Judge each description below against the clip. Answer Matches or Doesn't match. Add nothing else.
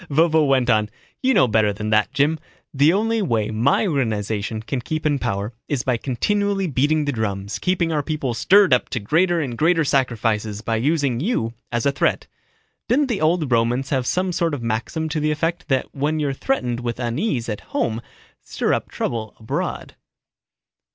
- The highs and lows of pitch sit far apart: Matches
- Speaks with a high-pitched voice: Doesn't match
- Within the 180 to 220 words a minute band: Matches